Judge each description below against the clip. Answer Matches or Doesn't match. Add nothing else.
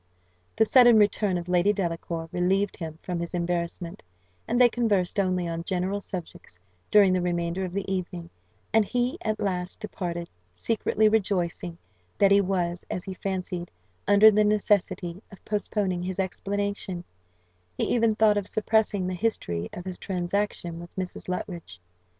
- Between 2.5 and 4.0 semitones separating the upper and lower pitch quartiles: Matches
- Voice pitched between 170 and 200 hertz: Matches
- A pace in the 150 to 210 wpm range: Matches